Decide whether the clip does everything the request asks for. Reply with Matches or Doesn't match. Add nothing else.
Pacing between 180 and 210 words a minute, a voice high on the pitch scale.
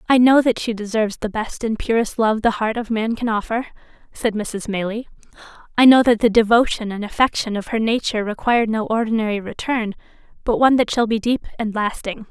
Matches